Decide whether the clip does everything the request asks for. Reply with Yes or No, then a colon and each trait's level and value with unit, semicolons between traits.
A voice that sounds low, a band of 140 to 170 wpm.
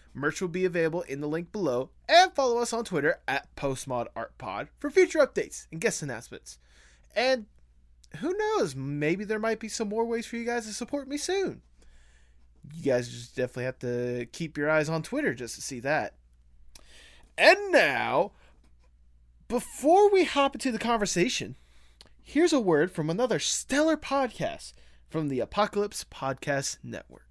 No: medium, 160 Hz; average, 160 wpm